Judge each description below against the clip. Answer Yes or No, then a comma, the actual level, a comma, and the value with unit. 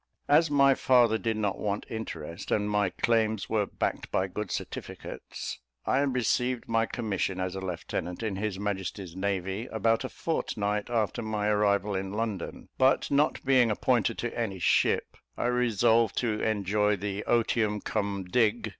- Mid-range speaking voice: No, low, 105 Hz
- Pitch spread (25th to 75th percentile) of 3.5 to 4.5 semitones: No, average, 2.8 semitones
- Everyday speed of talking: Yes, average, 155 wpm